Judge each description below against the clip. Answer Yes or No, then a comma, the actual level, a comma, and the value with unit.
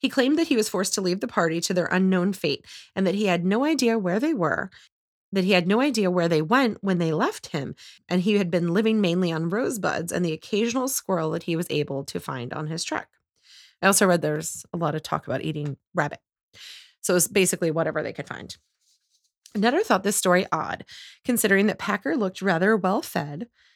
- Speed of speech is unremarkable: No, fast, 220 wpm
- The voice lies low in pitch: No, medium, 185 Hz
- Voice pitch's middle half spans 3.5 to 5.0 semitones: Yes, average, 4.1 semitones